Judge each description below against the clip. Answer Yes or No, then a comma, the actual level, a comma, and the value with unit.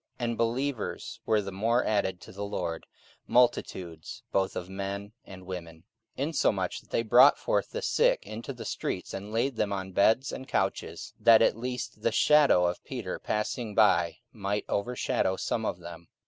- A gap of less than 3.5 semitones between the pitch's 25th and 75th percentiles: No, average, 3.8 semitones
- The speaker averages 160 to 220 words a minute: Yes, average, 180 wpm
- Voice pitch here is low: Yes, low, 105 Hz